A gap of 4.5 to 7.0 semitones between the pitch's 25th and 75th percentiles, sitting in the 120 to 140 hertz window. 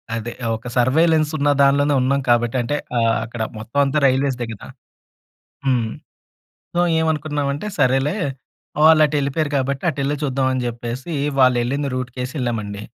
No: average, 3.2 semitones; low, 135 Hz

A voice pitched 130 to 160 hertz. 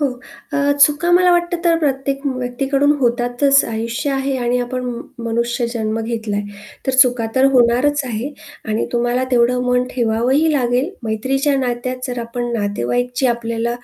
No: very high, 250 Hz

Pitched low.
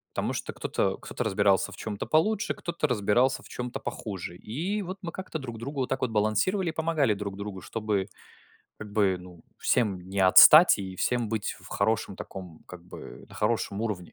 Yes: low, 110 Hz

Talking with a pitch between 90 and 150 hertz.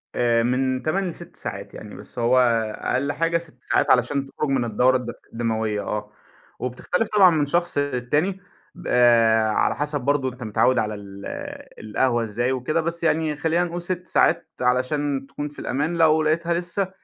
Yes: low, 135 Hz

